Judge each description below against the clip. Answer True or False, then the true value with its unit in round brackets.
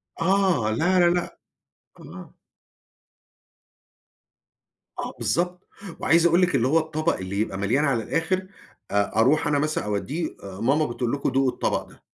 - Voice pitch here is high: False (150 Hz)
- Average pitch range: False (6.9 semitones)